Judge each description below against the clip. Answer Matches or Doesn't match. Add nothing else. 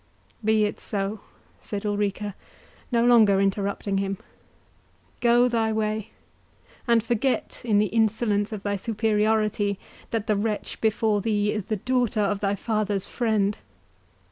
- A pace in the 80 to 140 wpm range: Matches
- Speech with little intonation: Matches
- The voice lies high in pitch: Matches